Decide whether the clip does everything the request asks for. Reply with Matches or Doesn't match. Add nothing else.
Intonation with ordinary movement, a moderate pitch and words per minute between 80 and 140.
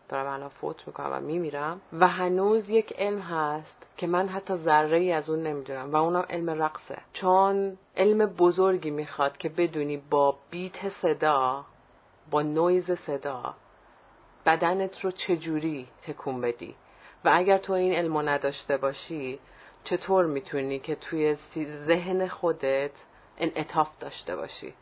Matches